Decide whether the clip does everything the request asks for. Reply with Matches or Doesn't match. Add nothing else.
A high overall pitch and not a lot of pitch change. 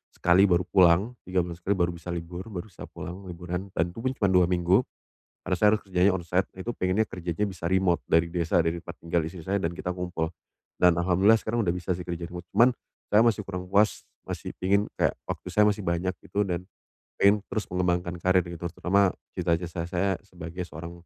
Doesn't match